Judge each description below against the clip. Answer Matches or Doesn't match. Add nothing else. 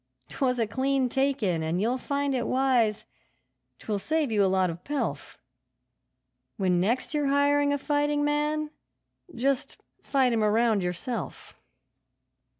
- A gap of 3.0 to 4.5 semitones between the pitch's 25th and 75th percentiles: Doesn't match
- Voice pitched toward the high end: Matches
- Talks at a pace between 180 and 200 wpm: Doesn't match